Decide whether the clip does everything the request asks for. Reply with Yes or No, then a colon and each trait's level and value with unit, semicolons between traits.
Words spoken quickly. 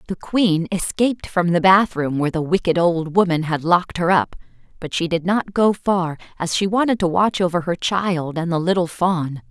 Yes: fast, 215 wpm